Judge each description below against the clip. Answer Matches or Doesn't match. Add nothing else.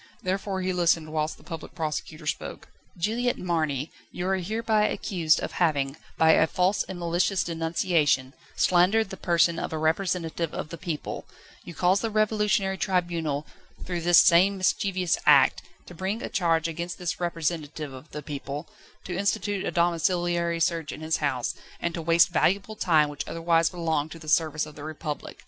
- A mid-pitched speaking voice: Matches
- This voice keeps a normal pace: Matches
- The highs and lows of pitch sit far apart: Doesn't match